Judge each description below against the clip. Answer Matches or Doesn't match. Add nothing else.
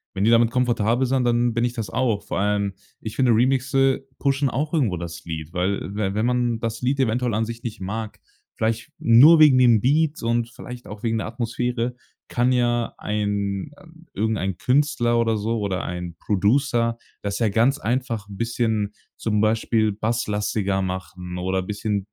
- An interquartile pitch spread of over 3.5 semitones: Doesn't match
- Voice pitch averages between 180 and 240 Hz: Doesn't match